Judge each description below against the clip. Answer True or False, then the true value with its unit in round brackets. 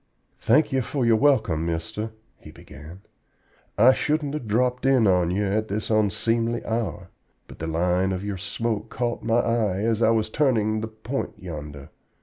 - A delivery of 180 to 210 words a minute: False (170 wpm)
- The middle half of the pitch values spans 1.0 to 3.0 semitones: False (4.4 semitones)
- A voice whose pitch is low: True (110 Hz)